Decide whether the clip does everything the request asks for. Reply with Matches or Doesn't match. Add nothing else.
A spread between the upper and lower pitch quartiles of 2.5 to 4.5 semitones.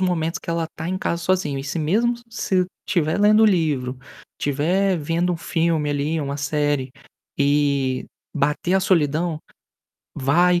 Matches